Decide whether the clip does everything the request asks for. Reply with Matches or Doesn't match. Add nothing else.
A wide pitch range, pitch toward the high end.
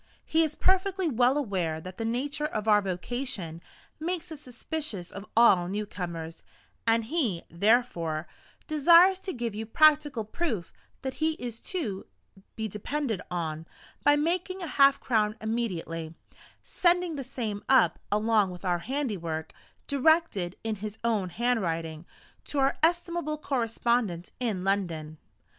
Matches